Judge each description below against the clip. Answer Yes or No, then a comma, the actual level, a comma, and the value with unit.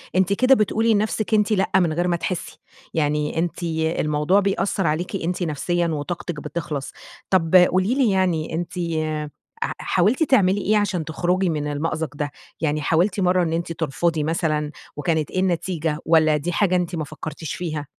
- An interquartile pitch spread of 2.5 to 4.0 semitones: Yes, average, 3.3 semitones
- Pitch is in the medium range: Yes, medium, 170 Hz